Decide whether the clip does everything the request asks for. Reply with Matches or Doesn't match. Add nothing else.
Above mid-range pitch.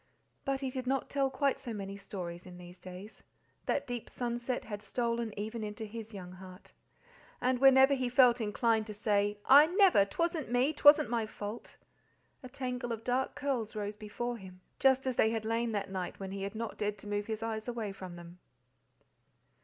Matches